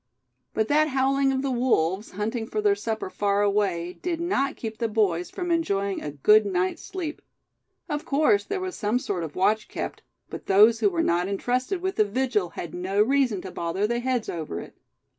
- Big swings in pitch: Yes, wide, 5.7 semitones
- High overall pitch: Yes, high, 220 Hz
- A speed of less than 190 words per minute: No, average, 195 wpm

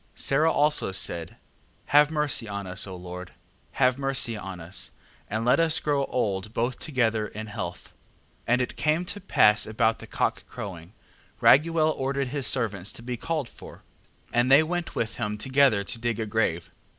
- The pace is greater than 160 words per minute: Yes, average, 175 wpm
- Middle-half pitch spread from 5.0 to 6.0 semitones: Yes, wide, 5.5 semitones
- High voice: No, low, 120 Hz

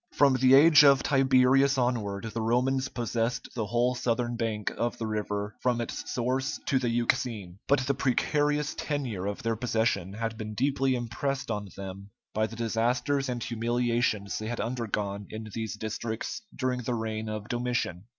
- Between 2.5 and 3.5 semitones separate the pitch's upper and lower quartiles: Yes, average, 2.9 semitones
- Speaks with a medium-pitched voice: No, low, 120 Hz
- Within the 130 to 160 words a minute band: No, average, 170 wpm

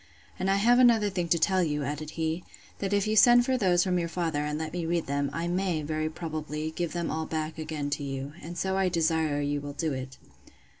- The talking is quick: Yes, fast, 240 wpm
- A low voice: No, medium, 160 Hz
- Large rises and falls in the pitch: No, average, 3.4 semitones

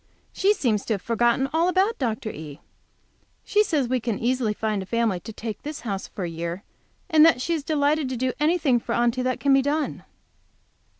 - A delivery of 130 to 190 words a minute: No, fast, 205 wpm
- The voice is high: Yes, very high, 250 Hz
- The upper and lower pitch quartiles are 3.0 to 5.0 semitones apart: No, wide, 5.6 semitones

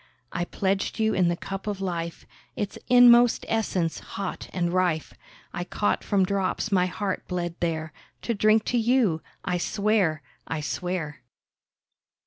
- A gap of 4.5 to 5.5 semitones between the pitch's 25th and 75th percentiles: No, average, 3.6 semitones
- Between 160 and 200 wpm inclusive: No, average, 140 wpm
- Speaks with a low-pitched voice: No, medium, 185 Hz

